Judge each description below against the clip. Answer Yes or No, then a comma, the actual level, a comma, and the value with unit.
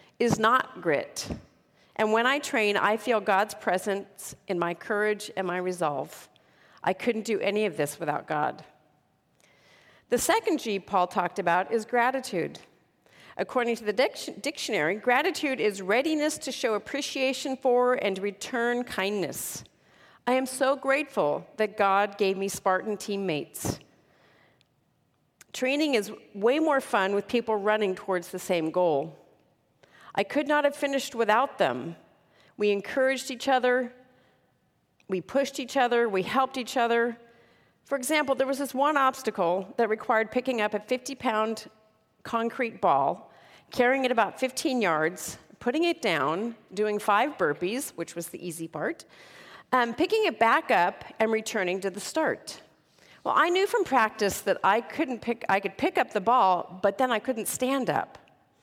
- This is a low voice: No, high, 225 Hz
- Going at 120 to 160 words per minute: Yes, average, 155 wpm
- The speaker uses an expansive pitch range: No, average, 4.9 semitones